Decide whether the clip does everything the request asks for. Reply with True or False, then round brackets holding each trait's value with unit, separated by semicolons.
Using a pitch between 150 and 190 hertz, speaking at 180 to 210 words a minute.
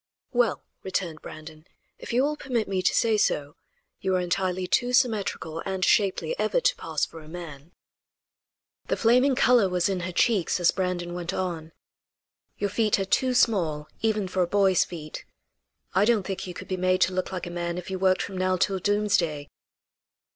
True (185 Hz; 190 wpm)